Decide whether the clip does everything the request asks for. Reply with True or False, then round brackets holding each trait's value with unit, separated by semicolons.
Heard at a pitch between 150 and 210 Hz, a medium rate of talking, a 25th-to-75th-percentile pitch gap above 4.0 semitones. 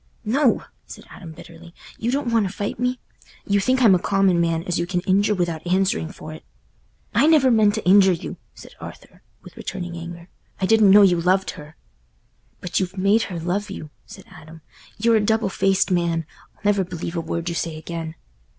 False (185 Hz; 195 wpm; 3.5 semitones)